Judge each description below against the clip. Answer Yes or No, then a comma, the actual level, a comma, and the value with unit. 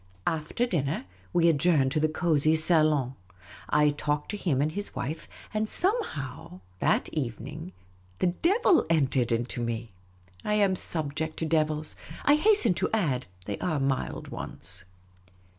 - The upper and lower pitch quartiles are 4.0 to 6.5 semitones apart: Yes, average, 4.6 semitones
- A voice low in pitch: No, medium, 155 Hz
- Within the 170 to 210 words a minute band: No, average, 140 wpm